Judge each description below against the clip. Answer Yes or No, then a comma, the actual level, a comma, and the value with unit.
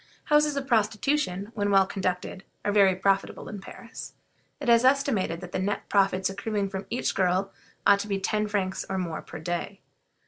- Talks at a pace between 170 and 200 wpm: Yes, average, 180 wpm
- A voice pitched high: Yes, high, 200 Hz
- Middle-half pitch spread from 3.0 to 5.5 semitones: No, narrow, 2.6 semitones